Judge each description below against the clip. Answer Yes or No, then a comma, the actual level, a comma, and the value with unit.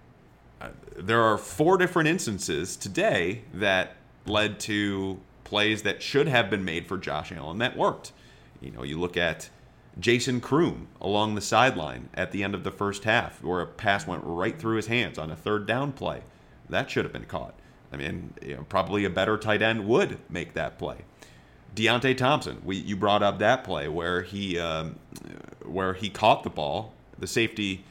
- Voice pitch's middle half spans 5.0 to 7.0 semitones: No, average, 3.5 semitones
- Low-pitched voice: Yes, low, 105 Hz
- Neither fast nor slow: Yes, average, 185 wpm